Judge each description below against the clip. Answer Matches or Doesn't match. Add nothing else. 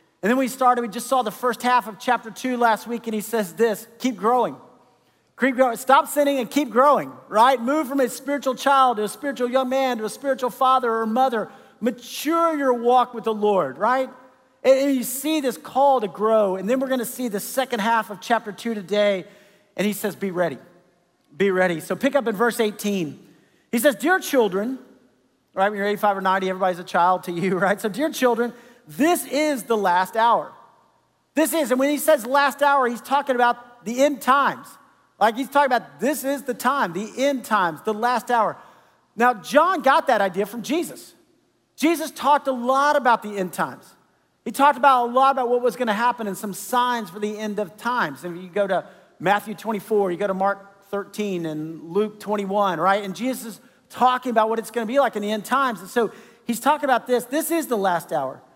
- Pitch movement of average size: Matches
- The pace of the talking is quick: Matches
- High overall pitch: Matches